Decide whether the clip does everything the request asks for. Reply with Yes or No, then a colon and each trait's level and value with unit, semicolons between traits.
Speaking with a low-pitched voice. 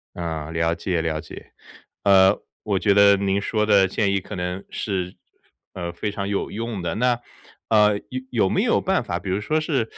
Yes: low, 100 Hz